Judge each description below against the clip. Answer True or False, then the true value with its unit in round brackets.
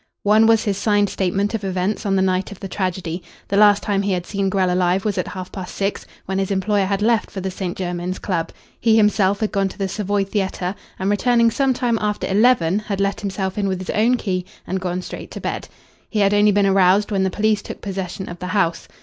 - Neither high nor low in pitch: False (195 Hz)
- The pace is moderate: False (240 wpm)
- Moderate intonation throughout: False (1.9 semitones)